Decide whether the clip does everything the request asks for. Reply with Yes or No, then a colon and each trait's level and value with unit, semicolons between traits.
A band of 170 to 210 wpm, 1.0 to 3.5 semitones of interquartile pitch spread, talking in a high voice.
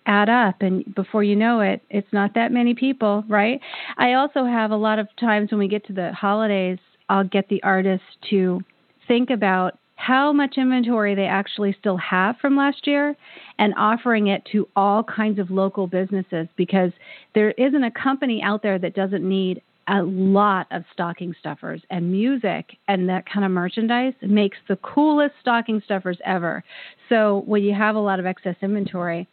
Yes: average, 185 wpm; average, 3.1 semitones; high, 205 Hz